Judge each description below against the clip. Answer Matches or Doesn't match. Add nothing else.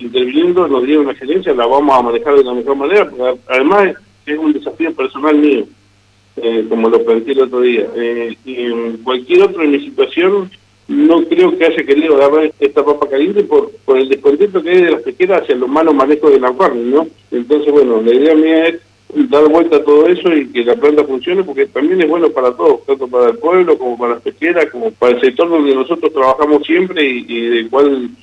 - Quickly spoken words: Matches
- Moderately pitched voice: Matches